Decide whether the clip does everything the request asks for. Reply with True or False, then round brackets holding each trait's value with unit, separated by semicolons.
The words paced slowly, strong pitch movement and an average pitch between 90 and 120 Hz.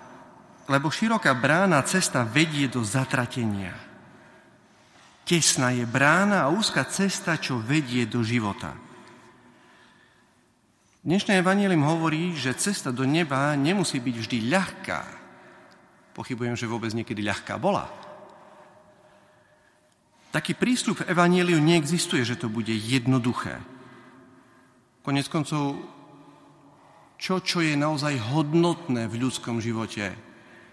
False (105 wpm; 5.9 semitones; 135 Hz)